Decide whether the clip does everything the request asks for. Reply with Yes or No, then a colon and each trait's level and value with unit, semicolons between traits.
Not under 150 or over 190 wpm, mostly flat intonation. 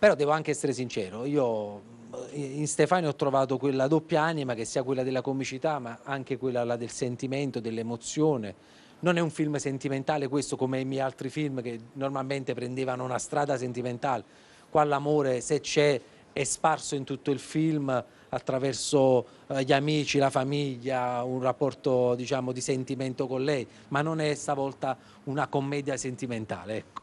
Yes: average, 160 wpm; narrow, 2.3 semitones